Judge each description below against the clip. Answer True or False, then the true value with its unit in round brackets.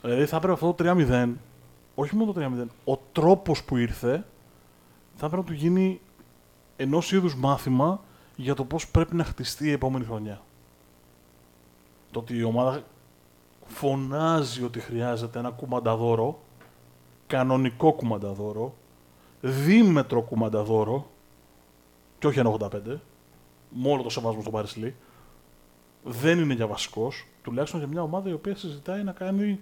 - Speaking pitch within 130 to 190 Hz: False (120 Hz)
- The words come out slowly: False (135 wpm)